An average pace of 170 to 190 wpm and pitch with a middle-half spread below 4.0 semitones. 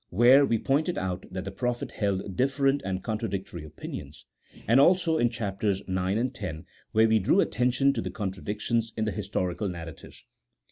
No: average, 180 wpm; average, 4.9 semitones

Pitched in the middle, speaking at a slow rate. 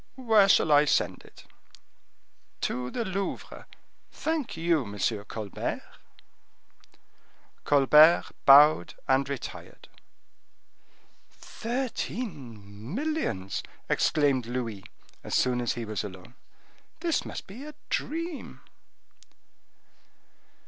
Yes: medium, 145 Hz; slow, 90 wpm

